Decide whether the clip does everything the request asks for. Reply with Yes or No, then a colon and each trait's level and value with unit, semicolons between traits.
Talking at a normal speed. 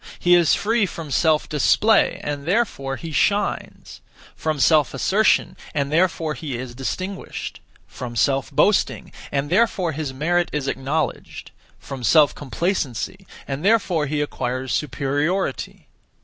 No: slow, 130 wpm